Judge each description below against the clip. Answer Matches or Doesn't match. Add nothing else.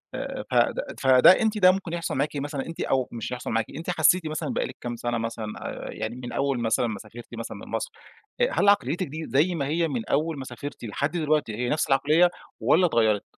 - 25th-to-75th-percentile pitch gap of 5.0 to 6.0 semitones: Matches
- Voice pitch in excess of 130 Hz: Matches